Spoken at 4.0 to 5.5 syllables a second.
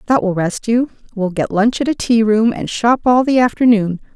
Yes: 5.0 syllables/s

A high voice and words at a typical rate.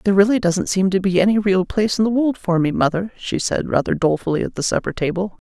No: high, 195 Hz; fast, 250 wpm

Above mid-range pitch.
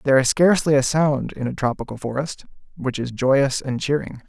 No: low, 135 Hz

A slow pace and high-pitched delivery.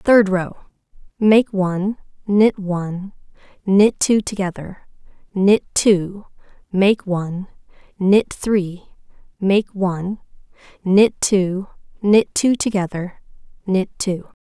Yes: slow, 95 wpm; high, 195 Hz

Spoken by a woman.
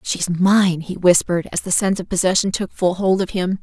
Yes: female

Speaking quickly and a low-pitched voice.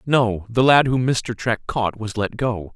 Yes: fast, 220 wpm; low, 115 Hz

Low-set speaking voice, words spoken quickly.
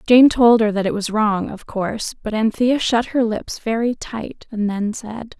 No: high, 220 Hz; fast, 210 wpm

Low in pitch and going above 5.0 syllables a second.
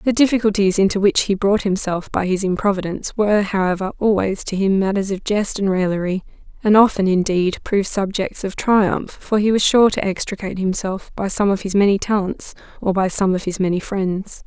No: high, 195 Hz; 5.5 syllables/s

